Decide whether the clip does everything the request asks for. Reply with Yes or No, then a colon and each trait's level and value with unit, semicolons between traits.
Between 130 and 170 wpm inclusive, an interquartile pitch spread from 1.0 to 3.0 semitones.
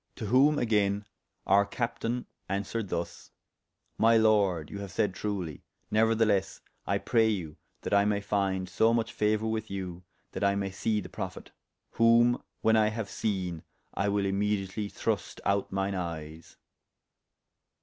Yes: average, 150 wpm; narrow, 2.4 semitones